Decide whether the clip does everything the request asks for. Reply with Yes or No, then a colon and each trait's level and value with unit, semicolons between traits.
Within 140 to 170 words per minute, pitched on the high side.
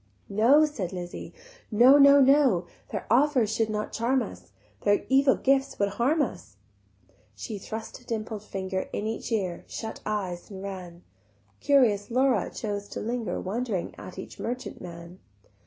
Yes: average, 155 wpm; high, 220 Hz